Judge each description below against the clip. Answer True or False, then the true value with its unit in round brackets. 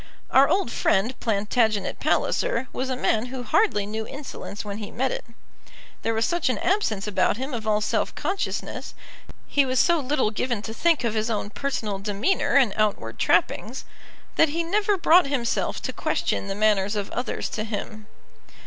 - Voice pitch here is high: True (230 Hz)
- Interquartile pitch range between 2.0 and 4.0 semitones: False (4.9 semitones)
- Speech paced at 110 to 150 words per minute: False (175 wpm)